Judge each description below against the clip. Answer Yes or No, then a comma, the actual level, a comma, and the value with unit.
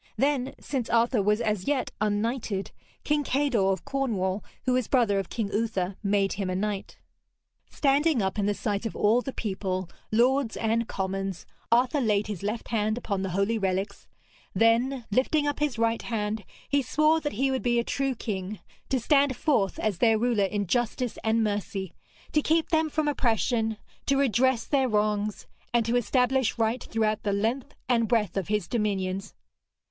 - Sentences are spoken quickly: No, average, 175 wpm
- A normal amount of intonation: Yes, average, 4.1 semitones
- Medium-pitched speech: No, high, 225 Hz